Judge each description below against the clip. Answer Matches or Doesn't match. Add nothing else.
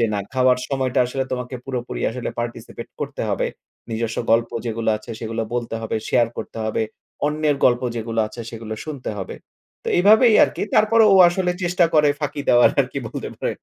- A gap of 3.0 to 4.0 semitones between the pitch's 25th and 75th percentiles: Doesn't match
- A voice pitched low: Matches